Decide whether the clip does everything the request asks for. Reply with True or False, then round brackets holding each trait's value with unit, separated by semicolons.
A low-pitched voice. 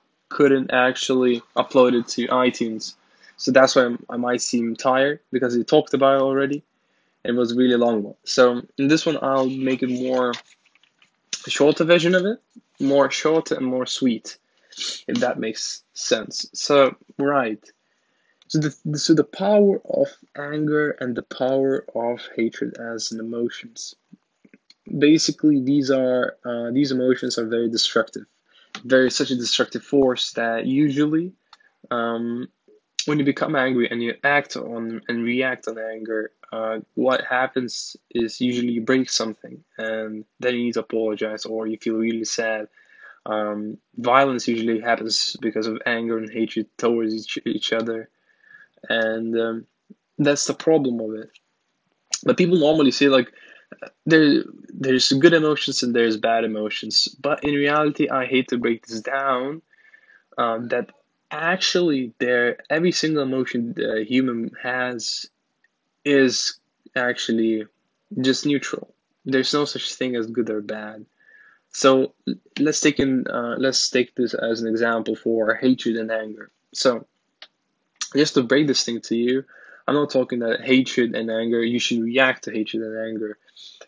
True (125 Hz)